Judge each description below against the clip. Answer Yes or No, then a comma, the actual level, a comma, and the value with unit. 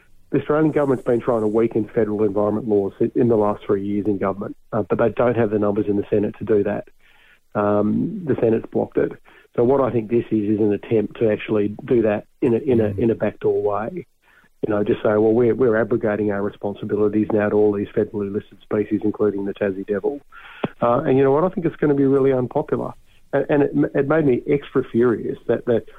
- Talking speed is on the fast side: Yes, fast, 230 wpm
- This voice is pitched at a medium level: No, low, 110 Hz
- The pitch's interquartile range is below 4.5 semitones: Yes, average, 2.8 semitones